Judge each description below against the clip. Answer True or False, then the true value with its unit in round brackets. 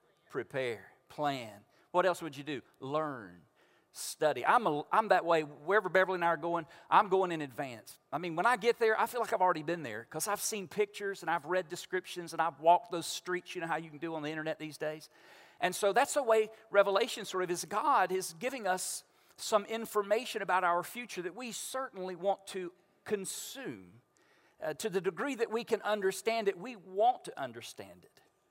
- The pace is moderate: False (210 wpm)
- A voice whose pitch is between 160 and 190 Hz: True (185 Hz)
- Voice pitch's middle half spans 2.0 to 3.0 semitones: False (4.3 semitones)